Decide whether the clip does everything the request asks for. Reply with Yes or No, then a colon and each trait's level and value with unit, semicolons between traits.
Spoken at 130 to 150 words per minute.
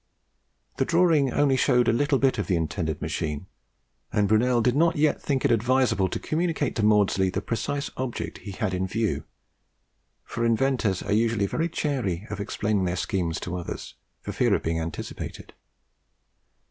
No: average, 170 wpm